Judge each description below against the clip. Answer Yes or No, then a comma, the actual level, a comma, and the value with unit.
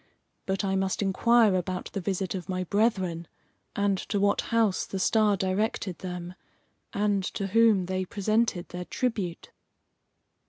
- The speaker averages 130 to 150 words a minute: Yes, average, 145 wpm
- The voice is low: No, high, 195 Hz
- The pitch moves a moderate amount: No, narrow, 2.2 semitones